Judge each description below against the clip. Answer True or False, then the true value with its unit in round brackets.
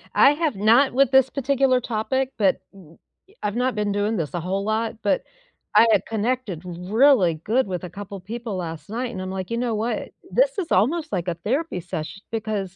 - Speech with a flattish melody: False (5.4 semitones)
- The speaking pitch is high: True (215 Hz)